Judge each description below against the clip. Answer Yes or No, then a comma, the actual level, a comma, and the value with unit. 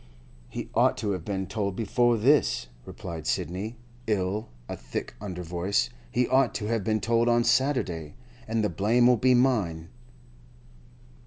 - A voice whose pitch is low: Yes, low, 105 Hz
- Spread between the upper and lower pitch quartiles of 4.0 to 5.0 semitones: Yes, average, 4.6 semitones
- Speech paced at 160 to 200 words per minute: No, average, 150 wpm